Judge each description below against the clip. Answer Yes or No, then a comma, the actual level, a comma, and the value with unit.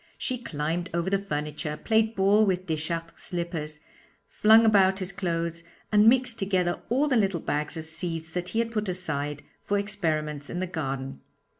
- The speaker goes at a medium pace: Yes, average, 170 wpm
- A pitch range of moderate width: Yes, average, 4.3 semitones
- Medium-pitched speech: Yes, medium, 180 Hz